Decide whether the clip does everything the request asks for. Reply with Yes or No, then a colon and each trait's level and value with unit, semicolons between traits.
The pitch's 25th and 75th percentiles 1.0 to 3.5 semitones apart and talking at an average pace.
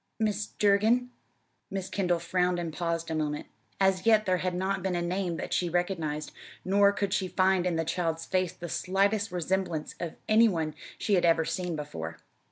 Yes: average, 2.8 semitones; average, 185 wpm